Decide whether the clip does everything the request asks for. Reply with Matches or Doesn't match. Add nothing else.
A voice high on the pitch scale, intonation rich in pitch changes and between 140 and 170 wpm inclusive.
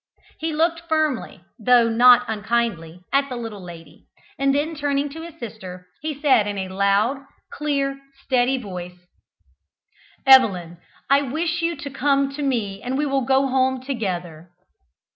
Matches